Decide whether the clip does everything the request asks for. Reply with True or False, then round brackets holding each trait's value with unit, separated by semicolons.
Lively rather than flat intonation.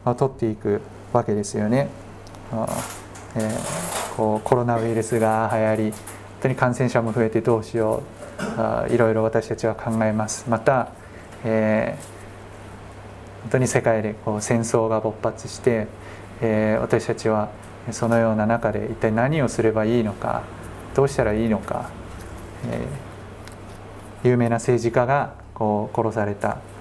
False (1.7 semitones)